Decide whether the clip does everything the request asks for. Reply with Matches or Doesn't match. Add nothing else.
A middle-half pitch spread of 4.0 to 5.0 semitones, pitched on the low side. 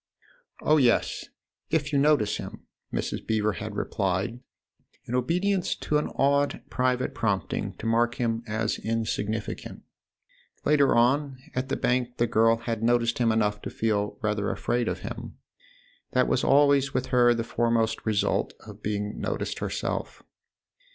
Doesn't match